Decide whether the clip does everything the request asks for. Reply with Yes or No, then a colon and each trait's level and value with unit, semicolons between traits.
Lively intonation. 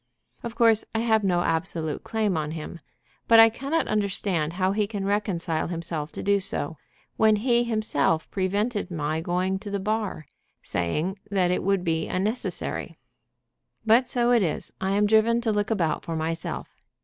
No: average, 4.7 semitones